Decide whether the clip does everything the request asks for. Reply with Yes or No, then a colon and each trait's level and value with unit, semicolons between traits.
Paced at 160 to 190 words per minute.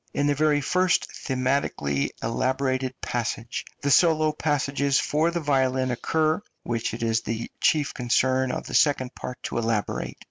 No: average, 150 wpm